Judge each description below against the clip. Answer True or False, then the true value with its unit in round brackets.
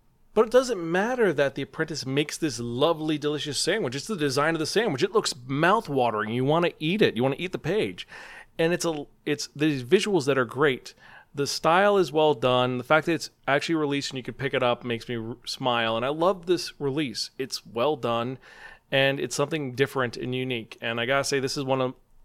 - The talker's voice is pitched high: False (140 Hz)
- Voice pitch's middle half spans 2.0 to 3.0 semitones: False (4.1 semitones)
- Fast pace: True (230 wpm)